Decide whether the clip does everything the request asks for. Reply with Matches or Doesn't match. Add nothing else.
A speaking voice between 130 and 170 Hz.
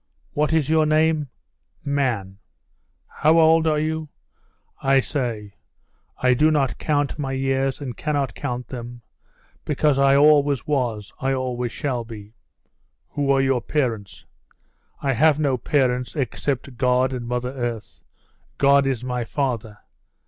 Matches